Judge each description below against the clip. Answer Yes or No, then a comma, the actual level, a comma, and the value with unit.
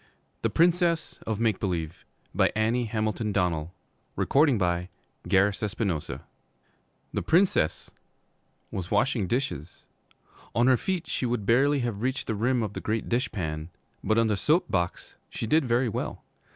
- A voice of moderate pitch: No, low, 110 Hz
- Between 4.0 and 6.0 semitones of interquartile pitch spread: Yes, average, 5.1 semitones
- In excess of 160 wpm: No, slow, 135 wpm